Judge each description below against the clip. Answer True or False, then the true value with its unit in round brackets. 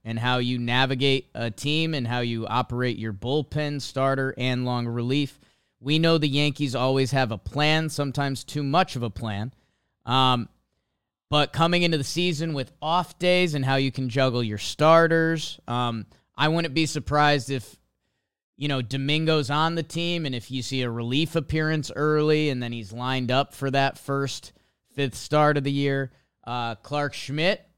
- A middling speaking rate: True (175 wpm)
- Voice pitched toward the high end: False (135 Hz)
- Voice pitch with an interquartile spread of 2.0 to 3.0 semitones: False (3.4 semitones)